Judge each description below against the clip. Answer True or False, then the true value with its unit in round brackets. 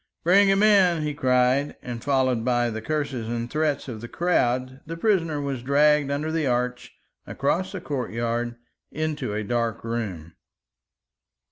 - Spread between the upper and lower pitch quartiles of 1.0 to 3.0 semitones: False (4.5 semitones)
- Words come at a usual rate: True (150 wpm)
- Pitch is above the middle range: False (130 Hz)